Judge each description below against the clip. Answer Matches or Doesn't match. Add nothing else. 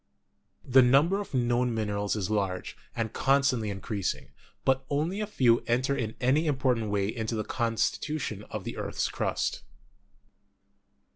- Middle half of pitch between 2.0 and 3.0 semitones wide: Doesn't match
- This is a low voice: Matches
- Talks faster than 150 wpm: Doesn't match